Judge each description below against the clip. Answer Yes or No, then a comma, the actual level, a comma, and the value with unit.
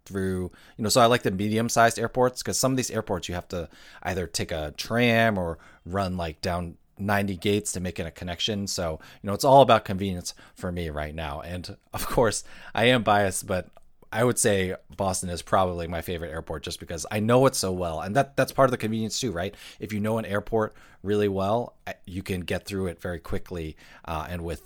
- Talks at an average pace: No, fast, 225 wpm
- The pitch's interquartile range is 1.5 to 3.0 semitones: No, average, 3.9 semitones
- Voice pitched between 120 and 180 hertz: No, very low, 95 Hz